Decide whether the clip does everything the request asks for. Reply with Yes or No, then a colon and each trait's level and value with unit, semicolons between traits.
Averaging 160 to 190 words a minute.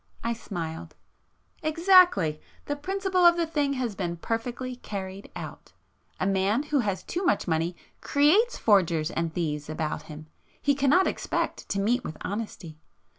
No: average, 145 wpm